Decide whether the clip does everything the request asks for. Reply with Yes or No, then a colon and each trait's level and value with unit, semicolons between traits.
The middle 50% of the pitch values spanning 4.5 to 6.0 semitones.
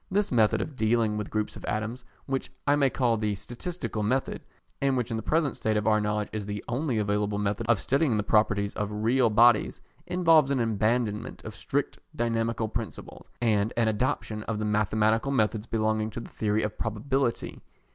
No: average, 2.7 semitones